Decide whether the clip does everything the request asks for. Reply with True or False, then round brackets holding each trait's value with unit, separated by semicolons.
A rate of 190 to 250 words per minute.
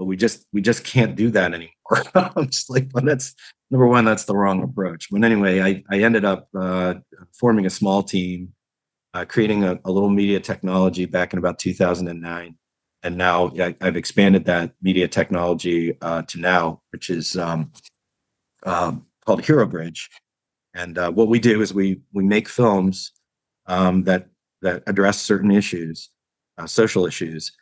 False (170 wpm)